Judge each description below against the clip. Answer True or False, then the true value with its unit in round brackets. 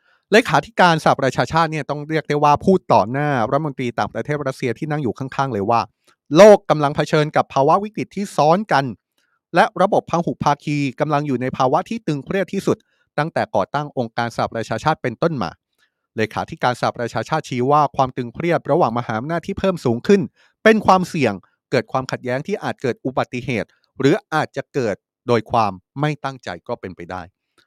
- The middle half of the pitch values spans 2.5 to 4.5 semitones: False (5.1 semitones)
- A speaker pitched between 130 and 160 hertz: True (140 Hz)